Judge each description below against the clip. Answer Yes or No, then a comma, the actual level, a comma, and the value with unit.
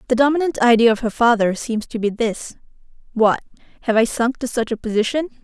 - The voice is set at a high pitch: Yes, high, 235 Hz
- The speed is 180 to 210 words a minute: Yes, average, 200 wpm